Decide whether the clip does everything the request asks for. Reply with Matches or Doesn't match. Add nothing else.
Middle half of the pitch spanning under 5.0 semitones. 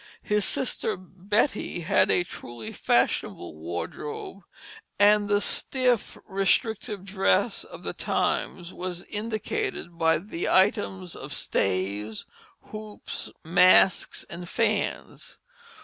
Matches